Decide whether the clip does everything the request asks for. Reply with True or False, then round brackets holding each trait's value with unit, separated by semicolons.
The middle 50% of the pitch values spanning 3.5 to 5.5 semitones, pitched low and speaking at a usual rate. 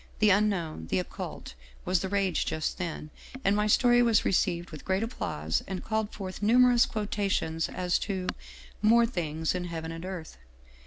False (4.3 semitones; 190 Hz; 170 wpm)